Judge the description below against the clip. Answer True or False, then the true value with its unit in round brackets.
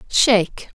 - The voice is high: True (215 Hz)